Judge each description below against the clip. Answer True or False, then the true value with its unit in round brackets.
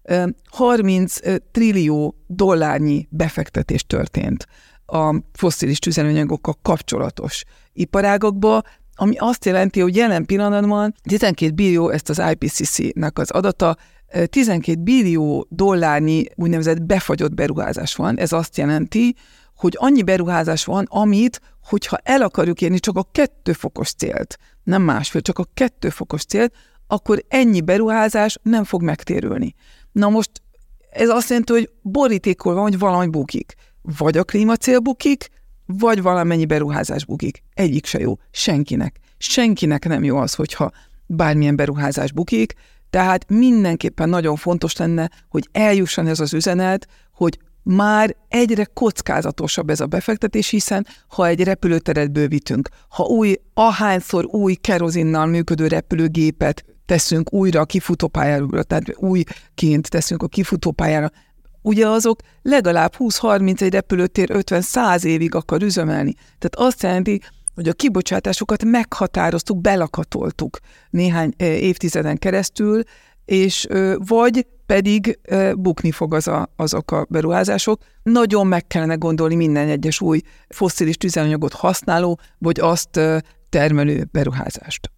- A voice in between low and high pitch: True (180 Hz)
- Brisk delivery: False (120 wpm)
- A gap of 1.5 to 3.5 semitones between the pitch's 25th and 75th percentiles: False (4.5 semitones)